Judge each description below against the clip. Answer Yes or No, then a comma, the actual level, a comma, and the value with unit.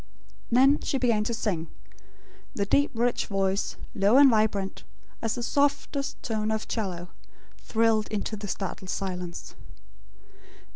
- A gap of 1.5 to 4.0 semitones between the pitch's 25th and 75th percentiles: Yes, average, 3.5 semitones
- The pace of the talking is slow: Yes, slow, 130 wpm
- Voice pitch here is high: Yes, high, 215 Hz